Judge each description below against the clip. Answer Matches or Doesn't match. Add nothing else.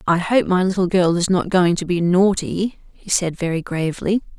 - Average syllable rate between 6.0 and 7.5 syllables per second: Doesn't match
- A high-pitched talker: Doesn't match